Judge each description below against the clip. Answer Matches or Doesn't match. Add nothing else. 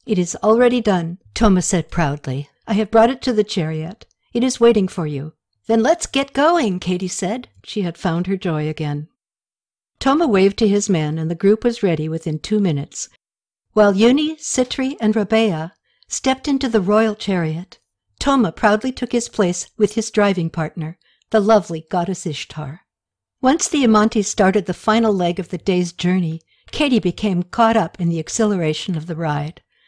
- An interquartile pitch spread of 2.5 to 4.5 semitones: Doesn't match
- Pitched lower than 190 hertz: Doesn't match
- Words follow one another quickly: Doesn't match